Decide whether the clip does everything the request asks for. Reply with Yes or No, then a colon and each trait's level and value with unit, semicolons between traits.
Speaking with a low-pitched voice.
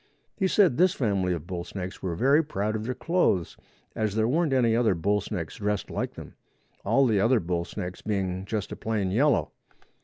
Yes: low, 105 Hz